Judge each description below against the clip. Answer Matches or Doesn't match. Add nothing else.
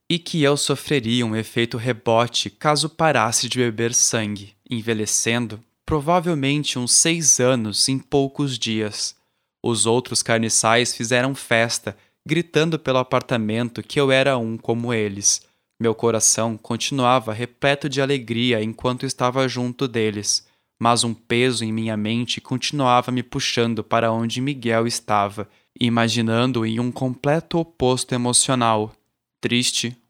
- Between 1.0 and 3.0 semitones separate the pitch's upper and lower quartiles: Matches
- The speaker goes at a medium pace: Matches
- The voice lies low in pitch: Matches